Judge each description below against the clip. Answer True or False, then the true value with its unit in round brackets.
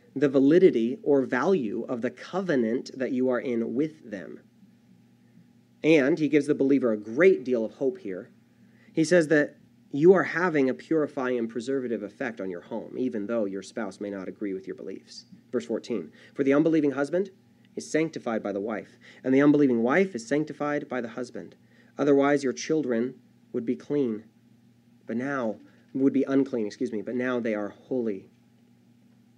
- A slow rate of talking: False (175 wpm)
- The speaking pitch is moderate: False (130 Hz)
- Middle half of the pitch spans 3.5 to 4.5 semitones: True (4.0 semitones)